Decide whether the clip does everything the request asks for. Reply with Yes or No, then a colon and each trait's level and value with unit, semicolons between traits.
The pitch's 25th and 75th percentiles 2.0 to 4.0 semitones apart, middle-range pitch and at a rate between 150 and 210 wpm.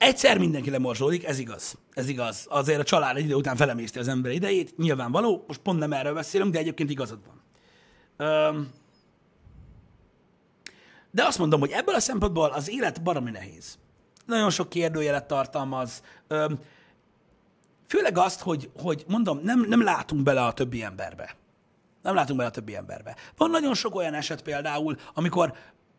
No: average, 4.7 semitones; medium, 150 Hz; fast, 155 wpm